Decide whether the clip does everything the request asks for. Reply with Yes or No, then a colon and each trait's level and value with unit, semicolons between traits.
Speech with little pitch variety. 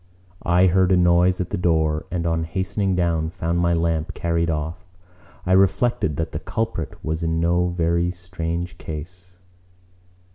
Yes: narrow, 1.7 semitones